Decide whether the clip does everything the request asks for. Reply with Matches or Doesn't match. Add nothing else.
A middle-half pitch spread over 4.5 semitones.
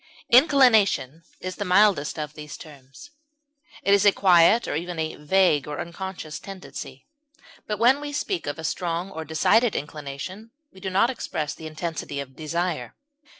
Matches